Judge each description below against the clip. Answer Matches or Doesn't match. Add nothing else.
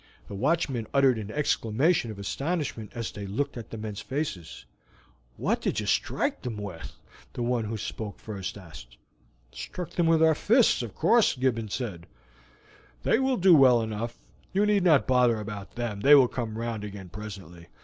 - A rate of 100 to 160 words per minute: Doesn't match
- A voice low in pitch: Matches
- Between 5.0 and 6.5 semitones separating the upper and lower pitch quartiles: Matches